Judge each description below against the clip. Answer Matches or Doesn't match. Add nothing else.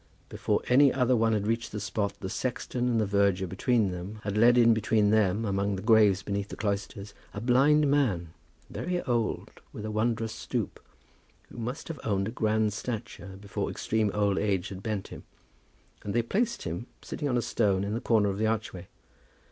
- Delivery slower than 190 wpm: Doesn't match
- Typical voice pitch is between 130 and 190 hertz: Doesn't match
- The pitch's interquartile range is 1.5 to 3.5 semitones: Matches